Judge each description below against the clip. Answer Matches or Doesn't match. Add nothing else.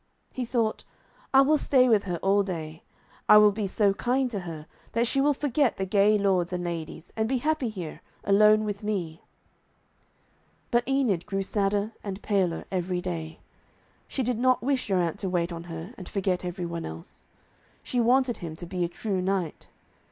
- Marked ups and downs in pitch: Doesn't match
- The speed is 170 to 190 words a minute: Matches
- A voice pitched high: Matches